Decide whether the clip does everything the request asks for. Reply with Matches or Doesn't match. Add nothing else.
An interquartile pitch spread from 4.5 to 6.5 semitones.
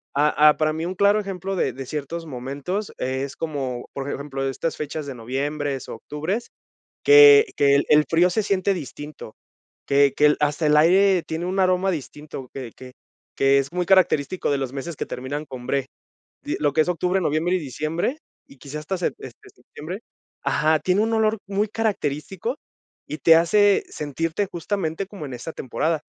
Matches